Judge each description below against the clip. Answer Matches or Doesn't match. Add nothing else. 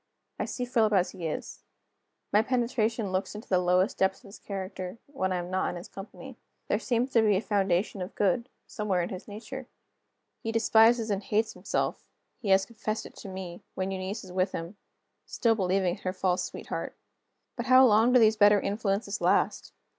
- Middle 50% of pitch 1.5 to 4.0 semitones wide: Matches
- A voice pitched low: Doesn't match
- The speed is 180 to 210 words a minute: Matches